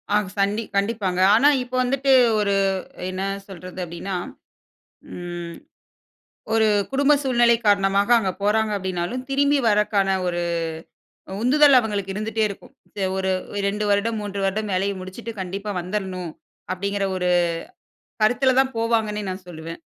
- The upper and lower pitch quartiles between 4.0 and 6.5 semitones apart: No, average, 3.4 semitones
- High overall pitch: Yes, high, 205 Hz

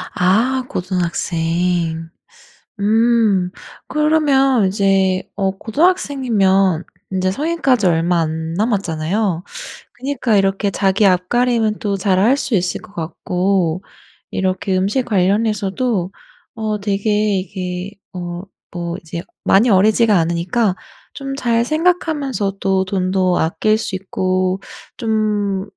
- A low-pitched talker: No, high, 195 Hz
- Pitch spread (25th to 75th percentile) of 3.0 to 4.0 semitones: Yes, average, 3.7 semitones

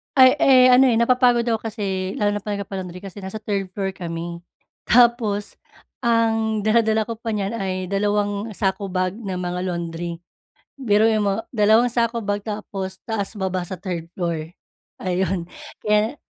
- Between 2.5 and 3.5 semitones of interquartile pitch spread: Yes, average, 3.1 semitones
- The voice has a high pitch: Yes, high, 205 Hz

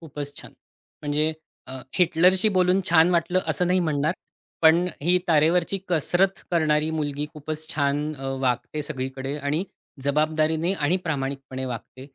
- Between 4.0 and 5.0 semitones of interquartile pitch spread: No, average, 3.4 semitones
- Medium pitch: Yes, medium, 155 Hz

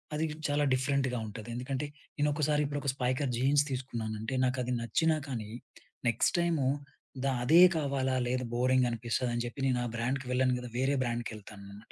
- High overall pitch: No, low, 130 Hz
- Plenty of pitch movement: No, average, 2.7 semitones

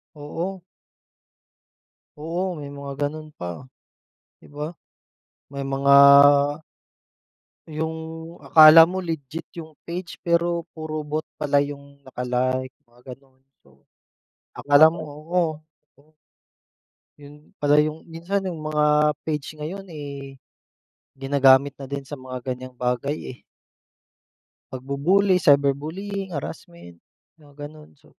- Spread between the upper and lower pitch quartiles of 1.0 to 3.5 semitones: Yes, average, 2.8 semitones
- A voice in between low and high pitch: Yes, medium, 150 Hz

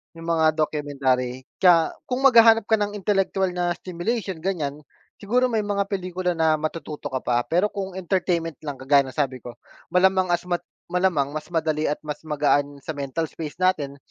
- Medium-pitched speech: Yes, medium, 165 Hz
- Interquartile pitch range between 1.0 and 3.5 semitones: No, average, 4.5 semitones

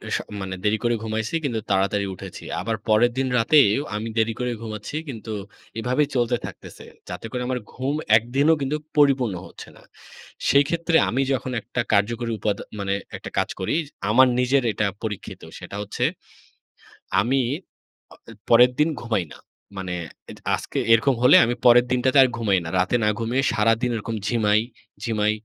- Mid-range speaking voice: No, low, 115 Hz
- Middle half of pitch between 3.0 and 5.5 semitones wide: Yes, average, 3.3 semitones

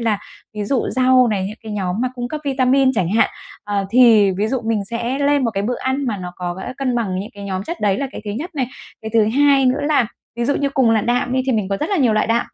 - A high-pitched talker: Yes, high, 235 Hz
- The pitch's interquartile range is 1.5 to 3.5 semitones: No, average, 4.3 semitones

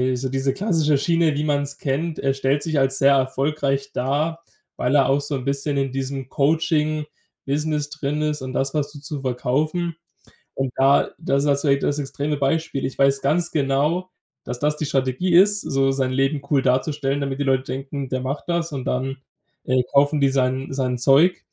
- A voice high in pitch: No, medium, 140 Hz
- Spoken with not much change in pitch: Yes, narrow, 2.0 semitones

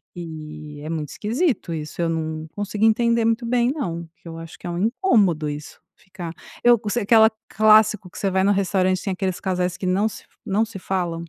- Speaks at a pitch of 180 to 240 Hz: Yes, high, 190 Hz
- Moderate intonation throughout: Yes, average, 4.8 semitones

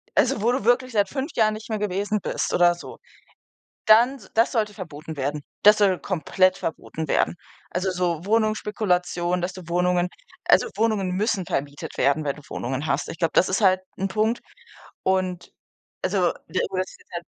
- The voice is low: No, medium, 185 Hz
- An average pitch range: Yes, average, 3.7 semitones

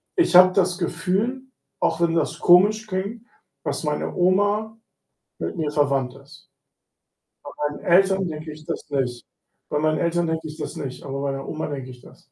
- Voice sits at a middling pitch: Yes, medium, 165 Hz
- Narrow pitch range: No, average, 4.5 semitones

